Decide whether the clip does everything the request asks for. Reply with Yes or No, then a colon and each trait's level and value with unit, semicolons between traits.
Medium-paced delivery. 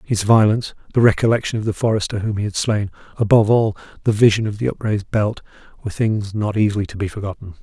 Yes: average, 195 wpm